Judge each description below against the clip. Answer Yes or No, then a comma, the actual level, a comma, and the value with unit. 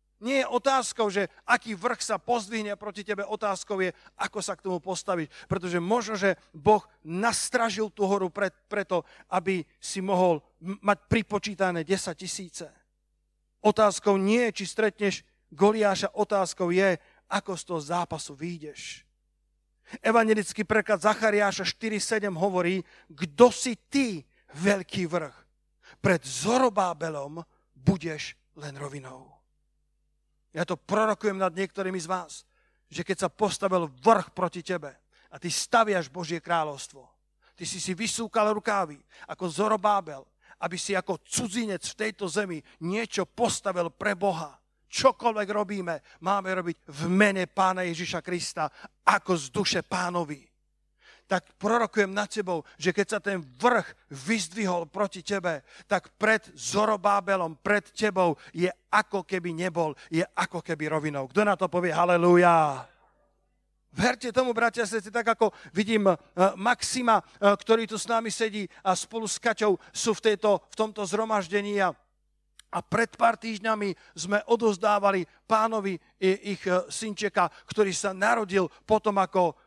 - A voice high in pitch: Yes, high, 195 Hz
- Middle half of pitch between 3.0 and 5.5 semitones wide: Yes, average, 3.5 semitones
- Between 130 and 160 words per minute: Yes, average, 135 wpm